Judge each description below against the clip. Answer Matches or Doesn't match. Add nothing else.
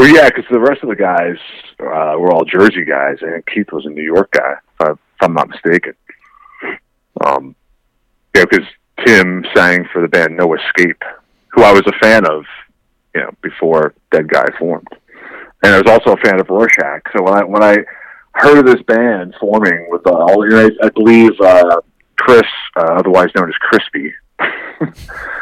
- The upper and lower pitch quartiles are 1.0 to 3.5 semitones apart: Doesn't match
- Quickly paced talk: Doesn't match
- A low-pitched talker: Matches